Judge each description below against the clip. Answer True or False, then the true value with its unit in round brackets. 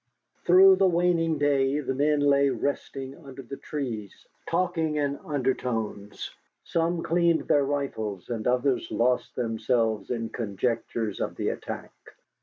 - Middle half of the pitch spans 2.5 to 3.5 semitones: False (4.7 semitones)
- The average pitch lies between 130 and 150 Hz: True (140 Hz)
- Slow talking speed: True (130 wpm)